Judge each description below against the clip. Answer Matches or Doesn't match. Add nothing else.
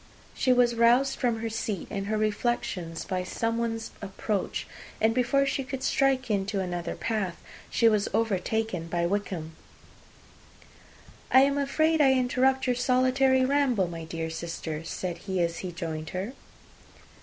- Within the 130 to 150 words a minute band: Matches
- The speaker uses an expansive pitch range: Matches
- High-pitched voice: Matches